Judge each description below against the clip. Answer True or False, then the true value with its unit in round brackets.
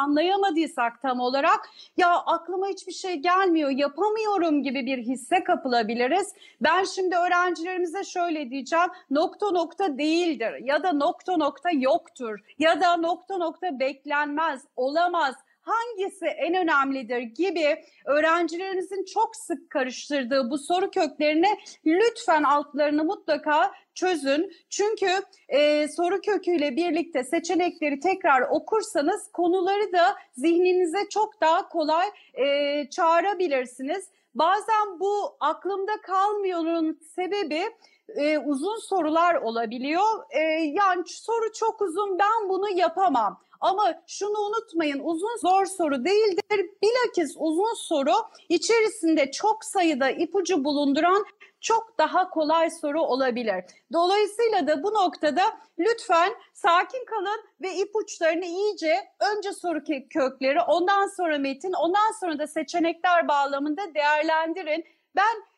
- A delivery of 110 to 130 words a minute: True (115 wpm)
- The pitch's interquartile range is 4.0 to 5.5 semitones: True (4.3 semitones)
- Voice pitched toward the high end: True (345 Hz)